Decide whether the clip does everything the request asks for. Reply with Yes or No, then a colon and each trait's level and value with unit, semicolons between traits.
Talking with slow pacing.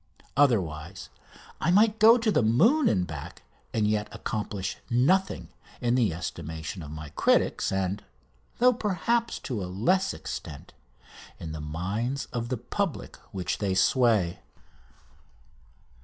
Yes: slow, 130 wpm